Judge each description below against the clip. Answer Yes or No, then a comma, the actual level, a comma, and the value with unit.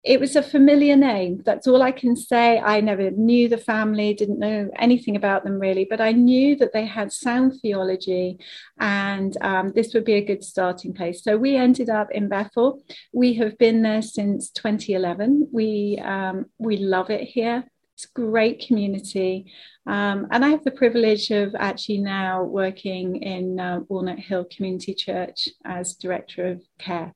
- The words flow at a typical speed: Yes, average, 175 wpm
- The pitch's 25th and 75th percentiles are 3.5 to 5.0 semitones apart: Yes, average, 3.9 semitones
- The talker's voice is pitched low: No, high, 210 Hz